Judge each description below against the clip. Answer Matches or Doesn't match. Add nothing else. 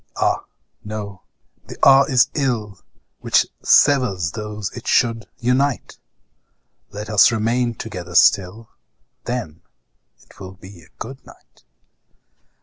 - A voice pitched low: Matches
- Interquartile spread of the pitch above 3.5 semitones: Matches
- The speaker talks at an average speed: Doesn't match